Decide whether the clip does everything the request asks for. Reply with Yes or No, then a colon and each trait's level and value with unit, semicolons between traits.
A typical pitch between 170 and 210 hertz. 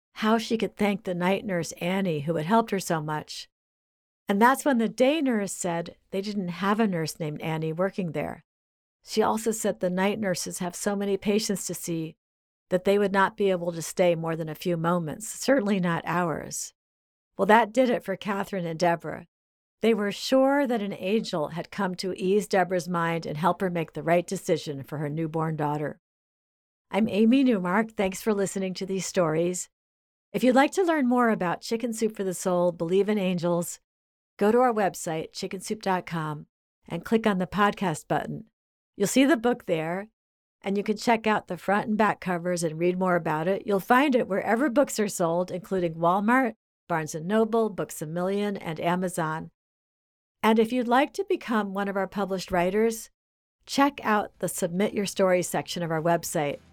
Yes: high, 190 Hz